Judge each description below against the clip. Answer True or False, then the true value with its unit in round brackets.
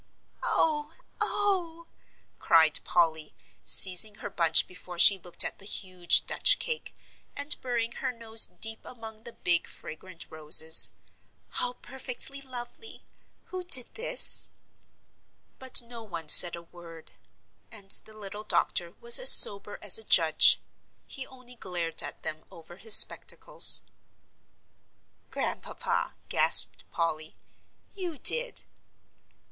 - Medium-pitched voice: False (215 Hz)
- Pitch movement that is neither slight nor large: False (7.3 semitones)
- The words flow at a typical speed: False (125 wpm)